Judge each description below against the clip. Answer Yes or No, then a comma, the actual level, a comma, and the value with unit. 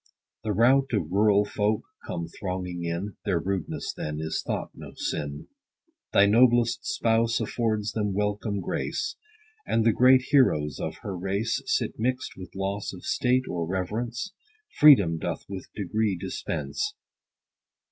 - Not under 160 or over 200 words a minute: No, average, 140 wpm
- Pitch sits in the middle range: No, low, 105 Hz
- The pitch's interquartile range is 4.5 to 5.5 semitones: No, average, 4.1 semitones